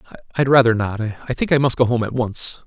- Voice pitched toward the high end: No, low, 120 Hz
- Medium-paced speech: No, fast, 225 wpm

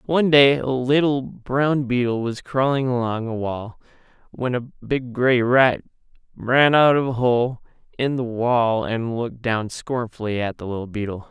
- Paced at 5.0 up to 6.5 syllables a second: No, 4.3 syllables/s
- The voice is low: Yes, low, 125 Hz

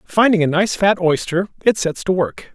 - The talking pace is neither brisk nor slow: No, fast, 210 wpm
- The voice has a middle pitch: Yes, medium, 180 Hz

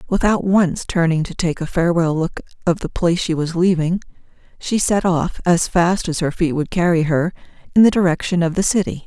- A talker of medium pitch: Yes, medium, 175 Hz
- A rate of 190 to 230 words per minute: Yes, fast, 205 wpm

